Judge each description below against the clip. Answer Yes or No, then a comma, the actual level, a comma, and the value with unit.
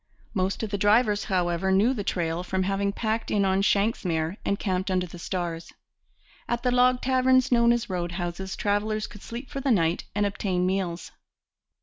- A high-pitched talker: Yes, high, 200 Hz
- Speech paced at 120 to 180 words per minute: No, average, 190 wpm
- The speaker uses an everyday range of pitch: Yes, average, 3.7 semitones